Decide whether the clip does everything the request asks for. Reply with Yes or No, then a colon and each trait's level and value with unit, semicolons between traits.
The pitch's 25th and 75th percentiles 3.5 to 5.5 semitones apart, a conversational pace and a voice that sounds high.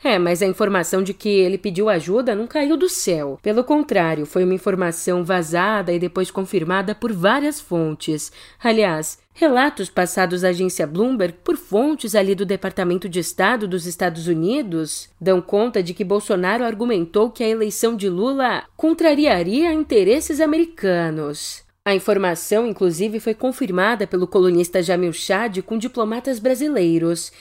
Yes: average, 4.4 semitones; average, 145 wpm; high, 195 Hz